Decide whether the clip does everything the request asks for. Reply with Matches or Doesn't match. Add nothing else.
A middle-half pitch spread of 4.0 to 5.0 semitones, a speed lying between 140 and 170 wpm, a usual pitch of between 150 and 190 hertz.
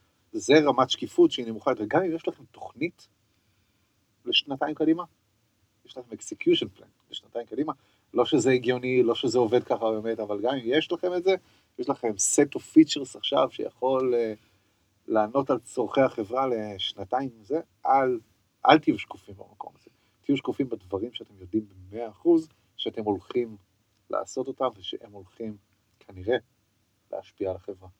Doesn't match